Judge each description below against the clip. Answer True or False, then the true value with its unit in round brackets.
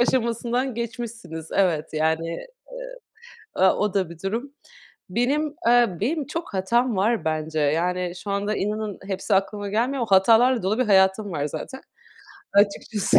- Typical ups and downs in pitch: True (4.6 semitones)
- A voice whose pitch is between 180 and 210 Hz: True (205 Hz)